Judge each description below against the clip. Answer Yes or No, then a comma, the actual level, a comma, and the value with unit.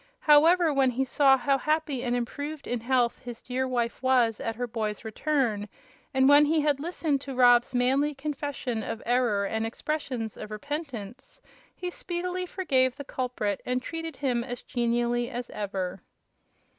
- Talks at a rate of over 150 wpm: Yes, average, 160 wpm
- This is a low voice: No, very high, 255 Hz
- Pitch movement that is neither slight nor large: Yes, average, 3.5 semitones